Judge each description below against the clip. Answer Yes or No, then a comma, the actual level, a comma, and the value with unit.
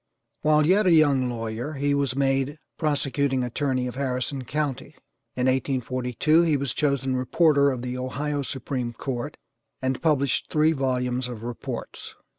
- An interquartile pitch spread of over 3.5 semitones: No, narrow, 2.4 semitones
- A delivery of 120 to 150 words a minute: Yes, average, 145 wpm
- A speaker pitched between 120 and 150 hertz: Yes, low, 135 Hz